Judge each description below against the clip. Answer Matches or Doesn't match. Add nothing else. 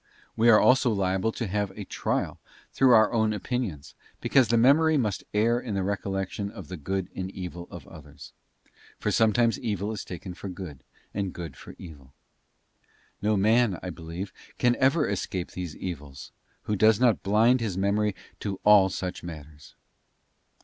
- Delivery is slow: Doesn't match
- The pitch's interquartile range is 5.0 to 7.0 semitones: Doesn't match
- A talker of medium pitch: Doesn't match